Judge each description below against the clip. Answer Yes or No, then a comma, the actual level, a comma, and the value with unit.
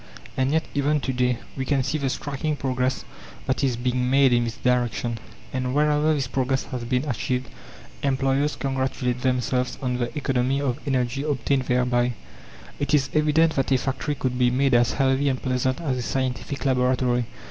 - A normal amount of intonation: No, narrow, 1.8 semitones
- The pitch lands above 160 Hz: No, low, 130 Hz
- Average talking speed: Yes, average, 180 wpm